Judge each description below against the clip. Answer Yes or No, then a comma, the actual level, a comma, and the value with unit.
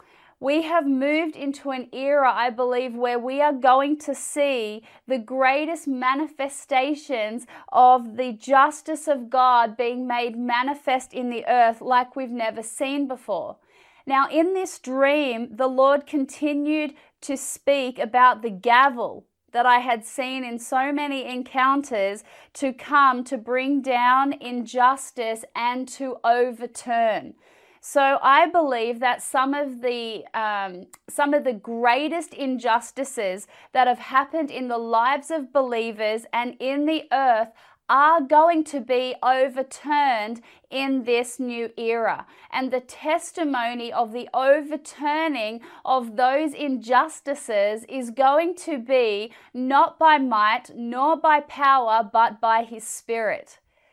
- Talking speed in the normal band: No, slow, 130 wpm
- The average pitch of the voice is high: Yes, very high, 260 Hz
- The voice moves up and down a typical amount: Yes, average, 3.2 semitones